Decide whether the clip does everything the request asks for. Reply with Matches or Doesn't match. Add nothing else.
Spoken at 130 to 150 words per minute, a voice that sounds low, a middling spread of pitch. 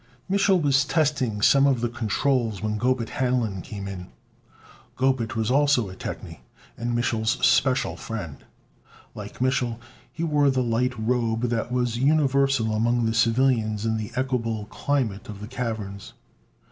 Matches